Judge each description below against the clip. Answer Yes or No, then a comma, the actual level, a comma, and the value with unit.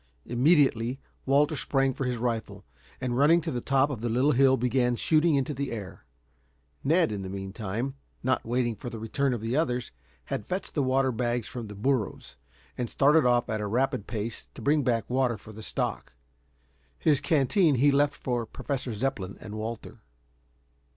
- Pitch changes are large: No, average, 3.3 semitones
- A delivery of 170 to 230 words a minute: Yes, average, 180 wpm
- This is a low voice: Yes, low, 125 Hz